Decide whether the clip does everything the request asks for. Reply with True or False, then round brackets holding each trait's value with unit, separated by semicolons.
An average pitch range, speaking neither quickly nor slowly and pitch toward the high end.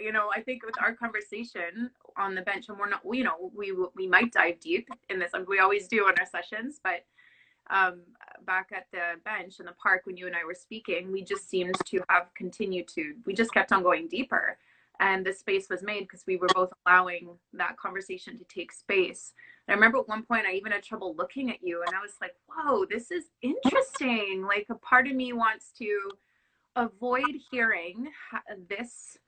False (4.4 semitones; 210 wpm; 205 Hz)